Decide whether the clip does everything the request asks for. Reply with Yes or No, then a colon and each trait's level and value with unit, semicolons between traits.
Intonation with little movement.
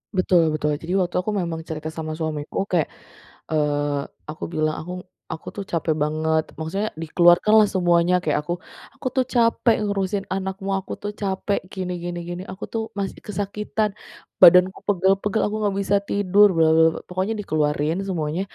No: average, 4.0 semitones